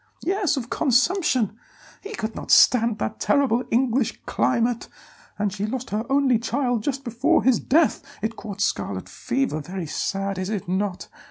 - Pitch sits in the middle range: No, high, 235 Hz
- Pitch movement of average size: Yes, average, 4.6 semitones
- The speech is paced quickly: No, average, 160 wpm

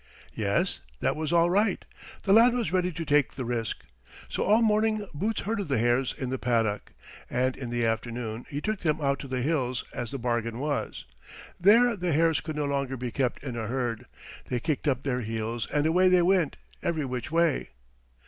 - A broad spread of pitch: Yes, wide, 6.1 semitones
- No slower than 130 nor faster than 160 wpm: No, average, 200 wpm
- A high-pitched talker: No, medium, 140 Hz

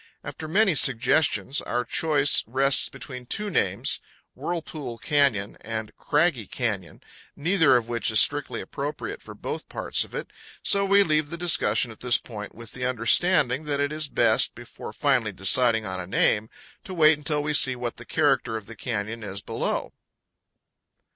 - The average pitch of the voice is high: No, low, 130 Hz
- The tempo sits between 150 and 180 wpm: Yes, average, 165 wpm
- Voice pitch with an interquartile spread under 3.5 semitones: No, average, 5.1 semitones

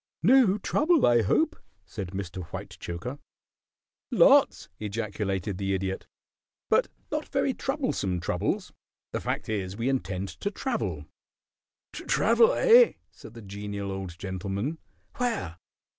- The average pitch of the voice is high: No, low, 100 Hz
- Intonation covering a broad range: Yes, wide, 7.2 semitones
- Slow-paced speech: Yes, slow, 120 wpm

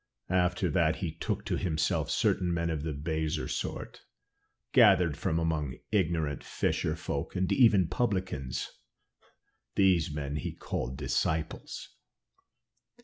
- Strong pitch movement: No, average, 3.2 semitones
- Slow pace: Yes, slow, 125 wpm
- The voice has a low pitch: Yes, very low, 80 Hz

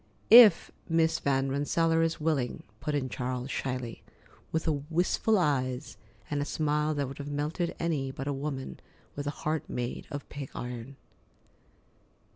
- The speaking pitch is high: No, medium, 145 Hz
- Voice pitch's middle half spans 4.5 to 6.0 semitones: No, average, 3.0 semitones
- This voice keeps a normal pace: Yes, average, 150 wpm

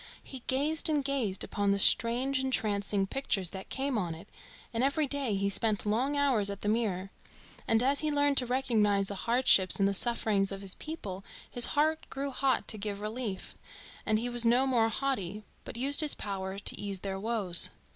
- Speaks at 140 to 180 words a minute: No, average, 195 wpm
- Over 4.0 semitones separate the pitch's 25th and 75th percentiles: Yes, average, 5.2 semitones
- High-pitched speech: Yes, high, 225 Hz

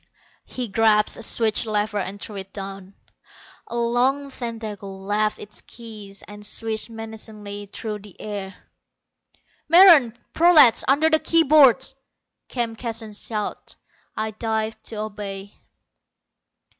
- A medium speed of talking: No, slow, 120 wpm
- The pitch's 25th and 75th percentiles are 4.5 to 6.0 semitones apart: No, narrow, 2.4 semitones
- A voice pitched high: Yes, high, 220 Hz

